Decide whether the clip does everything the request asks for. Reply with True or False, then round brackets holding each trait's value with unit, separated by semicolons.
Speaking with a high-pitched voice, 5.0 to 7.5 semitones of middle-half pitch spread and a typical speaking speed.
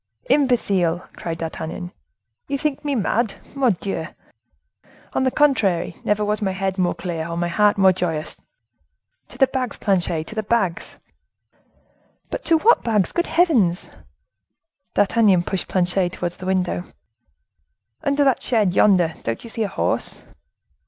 True (195 Hz; 5.5 semitones; 145 wpm)